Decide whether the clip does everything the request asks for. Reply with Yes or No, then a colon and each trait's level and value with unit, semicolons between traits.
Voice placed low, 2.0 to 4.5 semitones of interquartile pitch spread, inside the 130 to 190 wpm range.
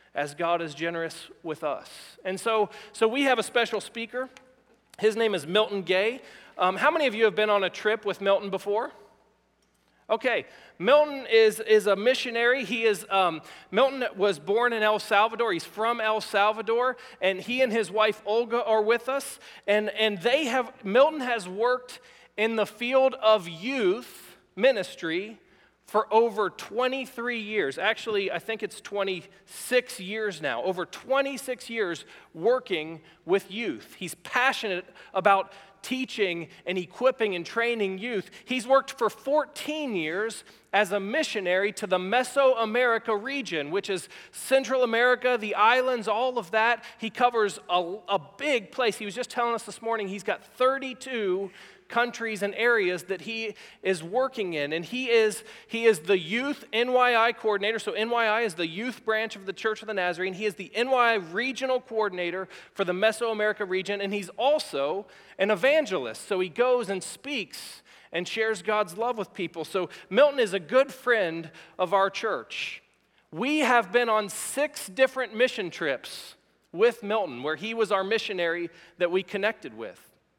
No: high, 220 Hz; average, 4.0 semitones; average, 165 wpm